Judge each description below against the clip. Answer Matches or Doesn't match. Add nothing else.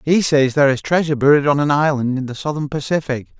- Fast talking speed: Matches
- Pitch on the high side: Doesn't match